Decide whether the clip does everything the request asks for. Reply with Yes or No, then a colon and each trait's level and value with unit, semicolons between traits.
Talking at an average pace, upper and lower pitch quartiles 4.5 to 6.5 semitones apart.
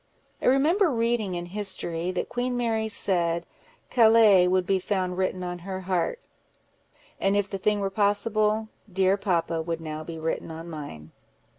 No: average, 160 wpm; average, 3.8 semitones